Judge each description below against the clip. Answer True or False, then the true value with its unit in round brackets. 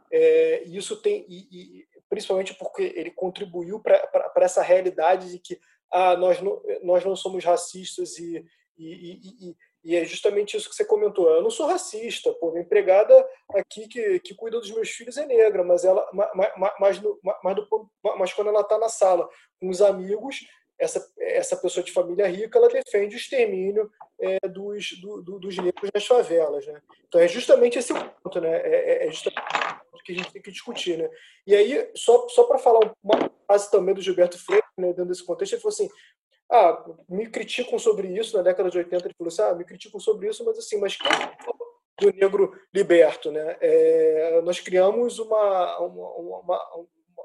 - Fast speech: True (190 wpm)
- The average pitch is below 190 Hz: False (235 Hz)